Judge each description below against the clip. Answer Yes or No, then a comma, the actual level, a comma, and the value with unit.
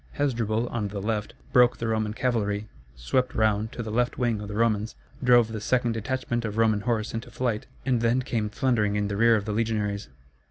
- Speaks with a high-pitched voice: No, low, 110 Hz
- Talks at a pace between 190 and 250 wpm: Yes, fast, 205 wpm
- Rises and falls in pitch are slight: Yes, narrow, 2.2 semitones